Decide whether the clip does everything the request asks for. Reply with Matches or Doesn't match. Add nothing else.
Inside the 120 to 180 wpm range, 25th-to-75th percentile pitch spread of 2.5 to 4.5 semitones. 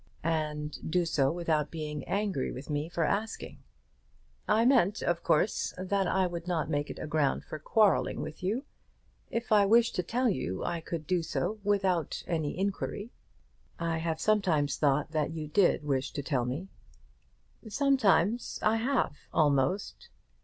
Doesn't match